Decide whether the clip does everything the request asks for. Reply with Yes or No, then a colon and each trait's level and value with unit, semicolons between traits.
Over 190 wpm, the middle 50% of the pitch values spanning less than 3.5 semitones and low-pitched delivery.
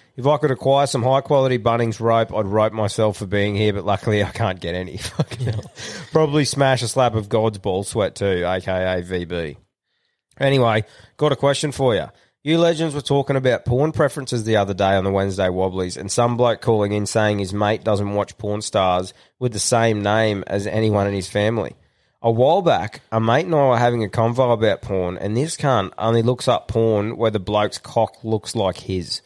No: fast, 205 wpm; average, 4.0 semitones; low, 110 Hz